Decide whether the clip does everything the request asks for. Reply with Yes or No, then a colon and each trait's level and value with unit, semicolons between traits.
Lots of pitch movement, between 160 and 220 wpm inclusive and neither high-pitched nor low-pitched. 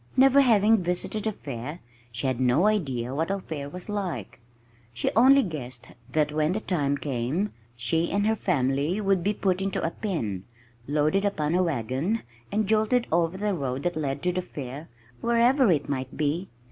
Yes: wide, 6.6 semitones; average, 180 wpm; medium, 170 Hz